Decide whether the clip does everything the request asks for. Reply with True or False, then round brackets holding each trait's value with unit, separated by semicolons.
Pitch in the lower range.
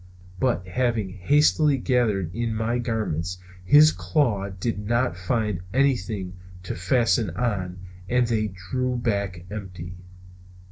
True (110 Hz)